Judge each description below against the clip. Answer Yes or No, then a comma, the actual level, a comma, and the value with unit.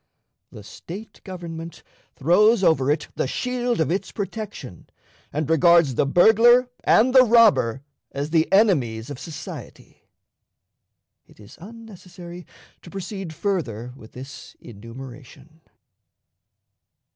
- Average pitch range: No, wide, 7.4 semitones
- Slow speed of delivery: Yes, slow, 110 wpm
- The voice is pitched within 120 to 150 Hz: No, medium, 170 Hz